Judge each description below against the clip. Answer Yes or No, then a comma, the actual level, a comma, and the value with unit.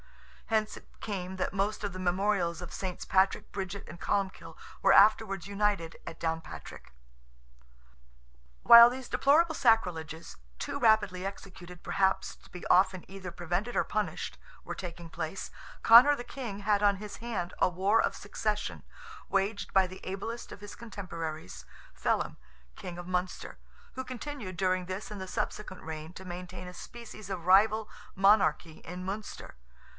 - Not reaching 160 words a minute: Yes, average, 150 wpm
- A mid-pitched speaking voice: No, high, 195 Hz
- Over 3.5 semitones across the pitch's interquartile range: No, average, 2.9 semitones